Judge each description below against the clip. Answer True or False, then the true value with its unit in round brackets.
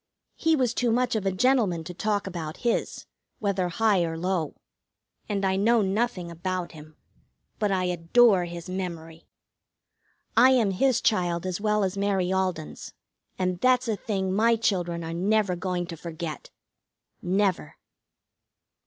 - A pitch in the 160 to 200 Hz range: True (190 Hz)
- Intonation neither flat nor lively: True (3.8 semitones)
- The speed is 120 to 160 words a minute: True (150 wpm)